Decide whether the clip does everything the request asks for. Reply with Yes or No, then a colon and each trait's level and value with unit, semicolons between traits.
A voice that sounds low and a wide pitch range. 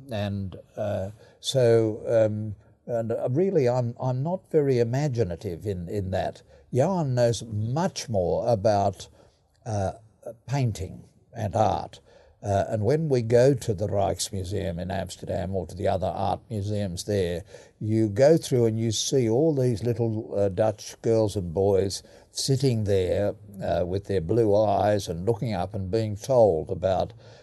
No: low, 110 Hz; average, 3.6 semitones